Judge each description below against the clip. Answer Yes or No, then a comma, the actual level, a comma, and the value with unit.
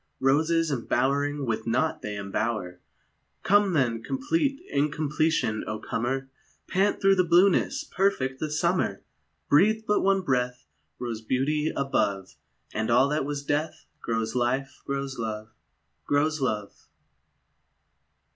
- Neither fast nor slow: No, slow, 120 wpm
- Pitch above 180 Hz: No, medium, 140 Hz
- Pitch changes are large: Yes, wide, 5.7 semitones